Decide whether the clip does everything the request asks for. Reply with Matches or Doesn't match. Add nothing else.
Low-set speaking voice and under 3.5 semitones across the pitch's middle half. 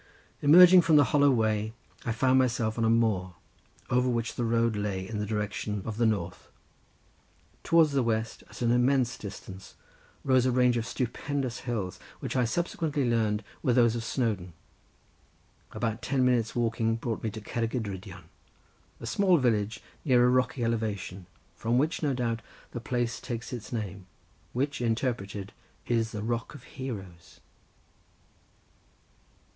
Matches